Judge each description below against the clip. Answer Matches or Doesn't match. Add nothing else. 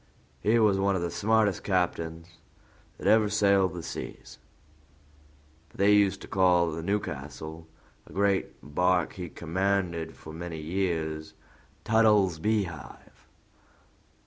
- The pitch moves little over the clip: Doesn't match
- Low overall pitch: Matches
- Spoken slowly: Matches